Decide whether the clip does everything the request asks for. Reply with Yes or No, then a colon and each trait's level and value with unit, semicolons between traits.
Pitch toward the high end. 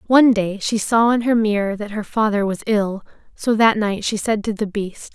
Yes: high, 215 Hz